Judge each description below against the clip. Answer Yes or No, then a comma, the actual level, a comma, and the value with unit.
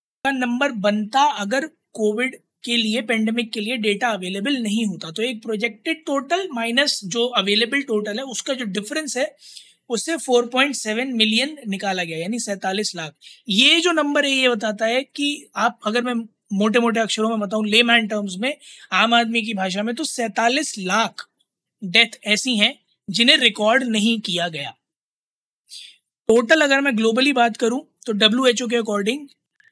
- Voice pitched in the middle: No, high, 235 Hz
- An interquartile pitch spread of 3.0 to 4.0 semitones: Yes, average, 3.7 semitones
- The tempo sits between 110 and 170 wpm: Yes, average, 160 wpm